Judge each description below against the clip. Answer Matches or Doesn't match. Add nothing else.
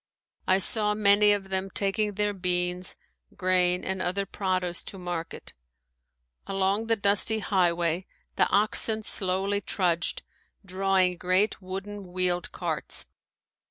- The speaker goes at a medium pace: Doesn't match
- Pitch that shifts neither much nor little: Doesn't match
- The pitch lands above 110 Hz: Matches